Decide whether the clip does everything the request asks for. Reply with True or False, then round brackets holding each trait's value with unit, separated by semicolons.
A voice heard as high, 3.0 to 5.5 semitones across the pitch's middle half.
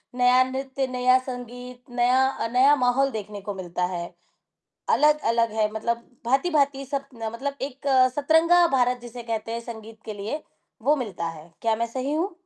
True (245 Hz; 3.4 semitones)